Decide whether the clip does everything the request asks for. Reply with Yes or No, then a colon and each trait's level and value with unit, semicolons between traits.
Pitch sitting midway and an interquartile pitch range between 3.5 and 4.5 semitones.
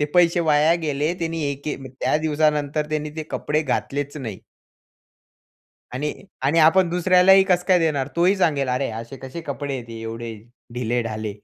Yes: medium, 150 Hz; average, 3.9 semitones